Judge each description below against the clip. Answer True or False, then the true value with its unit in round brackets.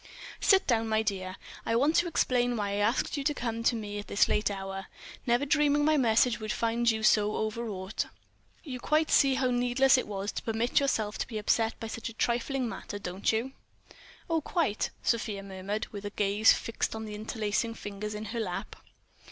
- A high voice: True (225 Hz)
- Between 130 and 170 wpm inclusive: False (195 wpm)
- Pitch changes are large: False (3.1 semitones)